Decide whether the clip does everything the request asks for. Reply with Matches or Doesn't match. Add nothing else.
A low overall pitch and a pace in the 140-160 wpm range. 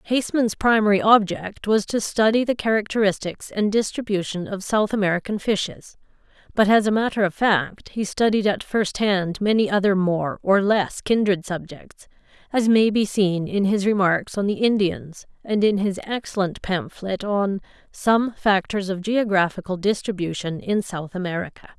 Doesn't match